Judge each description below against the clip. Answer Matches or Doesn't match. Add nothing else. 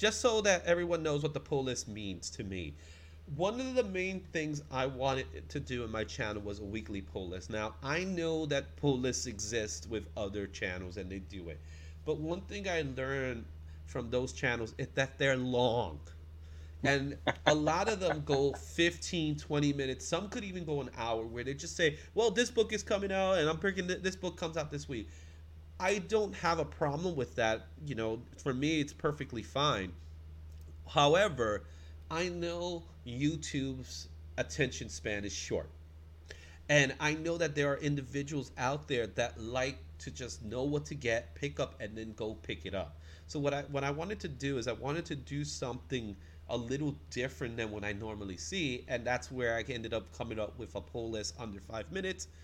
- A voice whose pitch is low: Matches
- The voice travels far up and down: Matches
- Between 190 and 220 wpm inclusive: Matches